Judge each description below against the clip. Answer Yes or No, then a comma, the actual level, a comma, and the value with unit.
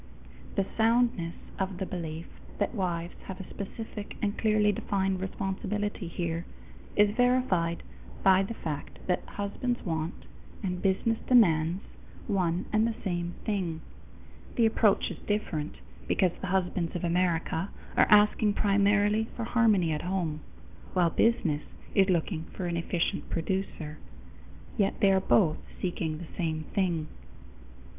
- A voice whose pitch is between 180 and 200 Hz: Yes, high, 190 Hz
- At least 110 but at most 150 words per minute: Yes, slow, 135 wpm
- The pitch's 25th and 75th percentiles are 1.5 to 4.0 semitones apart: Yes, average, 3.6 semitones